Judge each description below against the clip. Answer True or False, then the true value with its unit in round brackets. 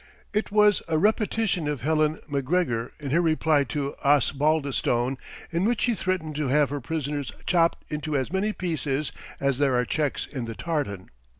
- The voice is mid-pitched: True (150 Hz)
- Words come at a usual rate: True (170 wpm)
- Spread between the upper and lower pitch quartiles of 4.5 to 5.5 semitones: False (3.6 semitones)